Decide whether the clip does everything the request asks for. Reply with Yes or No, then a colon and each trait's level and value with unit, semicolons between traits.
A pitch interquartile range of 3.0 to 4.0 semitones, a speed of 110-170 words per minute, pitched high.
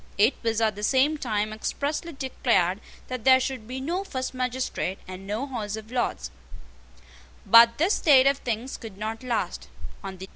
Yes: average, 3.7 semitones; average, 160 wpm; high, 240 Hz